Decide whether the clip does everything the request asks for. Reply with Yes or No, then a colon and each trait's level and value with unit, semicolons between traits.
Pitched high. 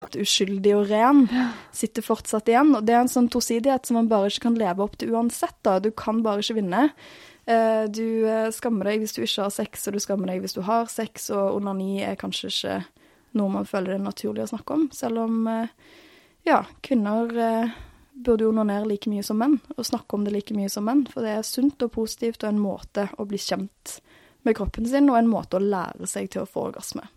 Yes: high, 220 Hz